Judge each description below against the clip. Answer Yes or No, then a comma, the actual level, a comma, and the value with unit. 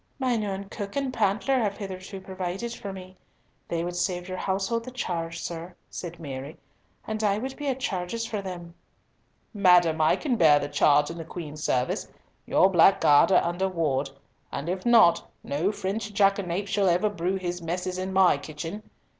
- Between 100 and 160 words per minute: No, average, 180 wpm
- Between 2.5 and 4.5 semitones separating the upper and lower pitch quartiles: Yes, average, 3.3 semitones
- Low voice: No, medium, 185 Hz